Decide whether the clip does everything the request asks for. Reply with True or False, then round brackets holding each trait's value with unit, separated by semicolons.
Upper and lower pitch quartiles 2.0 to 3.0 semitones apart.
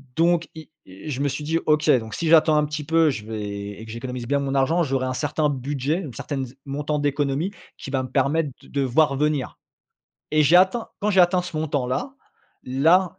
False (3.6 semitones)